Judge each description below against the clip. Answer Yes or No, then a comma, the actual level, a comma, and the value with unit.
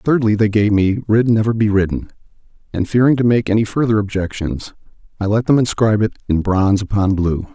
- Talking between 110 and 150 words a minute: No, average, 190 wpm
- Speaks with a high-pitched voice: No, low, 105 Hz